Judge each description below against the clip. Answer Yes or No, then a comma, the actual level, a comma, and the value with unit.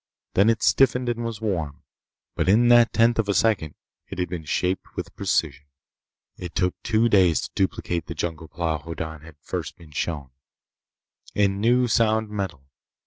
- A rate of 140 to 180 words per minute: Yes, average, 170 wpm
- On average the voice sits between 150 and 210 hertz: No, very low, 95 Hz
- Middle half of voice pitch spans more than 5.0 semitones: Yes, wide, 5.6 semitones